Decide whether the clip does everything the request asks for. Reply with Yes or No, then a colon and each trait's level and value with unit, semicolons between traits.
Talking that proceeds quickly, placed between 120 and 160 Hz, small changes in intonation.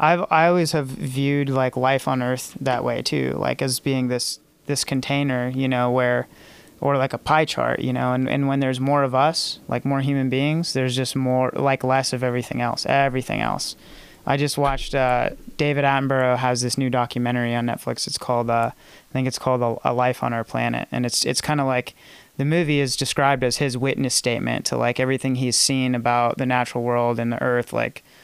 Yes: fast, 215 wpm; low, 130 Hz; narrow, 1.9 semitones